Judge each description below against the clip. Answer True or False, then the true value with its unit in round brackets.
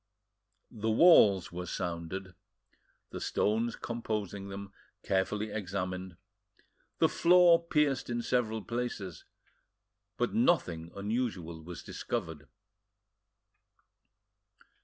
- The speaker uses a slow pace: True (85 wpm)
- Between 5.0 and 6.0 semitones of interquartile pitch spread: False (4.6 semitones)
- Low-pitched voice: True (100 Hz)